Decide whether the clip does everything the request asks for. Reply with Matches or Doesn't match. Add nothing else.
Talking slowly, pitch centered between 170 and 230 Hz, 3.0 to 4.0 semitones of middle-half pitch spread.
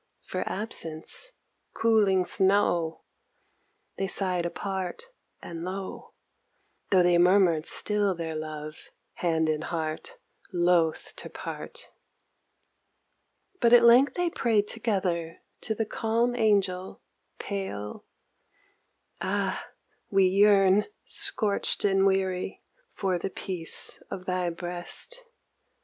Matches